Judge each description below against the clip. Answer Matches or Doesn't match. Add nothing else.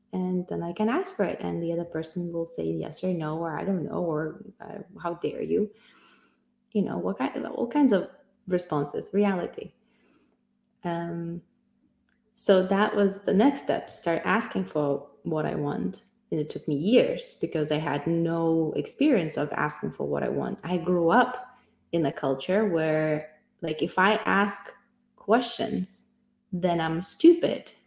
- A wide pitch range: Doesn't match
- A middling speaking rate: Matches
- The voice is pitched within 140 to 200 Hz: Matches